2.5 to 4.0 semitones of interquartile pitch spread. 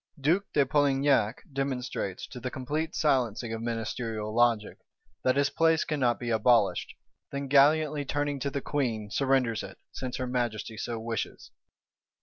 Yes: average, 3.6 semitones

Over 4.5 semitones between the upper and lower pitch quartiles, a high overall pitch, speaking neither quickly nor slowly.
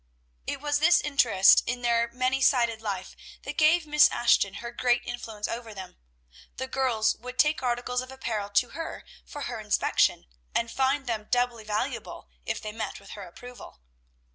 No: average, 3.2 semitones; high, 240 Hz; average, 170 wpm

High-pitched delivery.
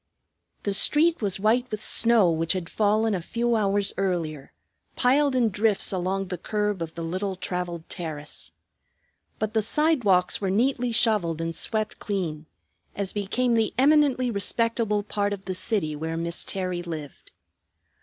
Yes: high, 200 Hz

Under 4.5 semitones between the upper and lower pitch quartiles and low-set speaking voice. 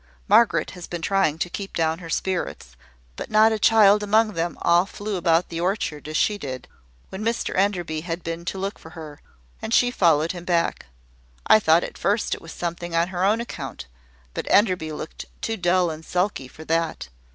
No: average, 3.7 semitones; medium, 175 Hz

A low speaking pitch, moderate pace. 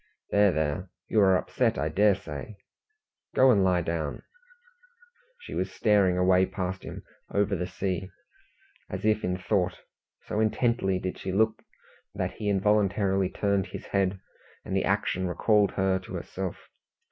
Yes: very low, 95 Hz; average, 150 wpm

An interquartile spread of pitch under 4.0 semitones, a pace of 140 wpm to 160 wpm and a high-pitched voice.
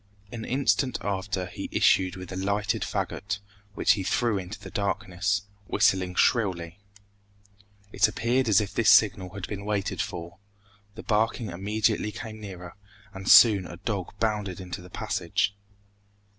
No: average, 2.7 semitones; average, 145 wpm; low, 100 Hz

